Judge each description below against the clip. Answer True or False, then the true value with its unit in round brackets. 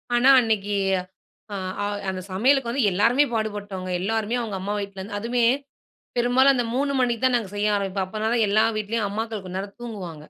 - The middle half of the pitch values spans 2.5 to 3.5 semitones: True (3.2 semitones)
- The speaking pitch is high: True (215 Hz)